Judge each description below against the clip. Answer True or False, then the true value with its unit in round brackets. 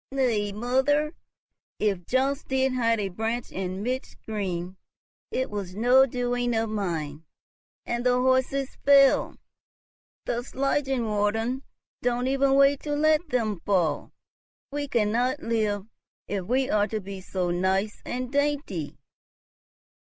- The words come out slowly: True (125 wpm)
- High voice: True (240 Hz)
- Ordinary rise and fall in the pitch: True (4.5 semitones)